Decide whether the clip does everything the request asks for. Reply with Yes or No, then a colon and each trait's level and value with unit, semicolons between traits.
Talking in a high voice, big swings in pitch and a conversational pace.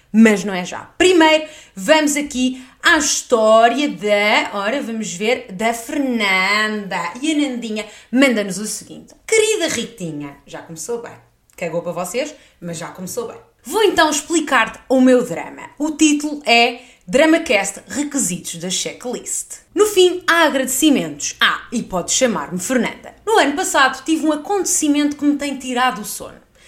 Yes: very high, 255 Hz; wide, 6.7 semitones; average, 150 wpm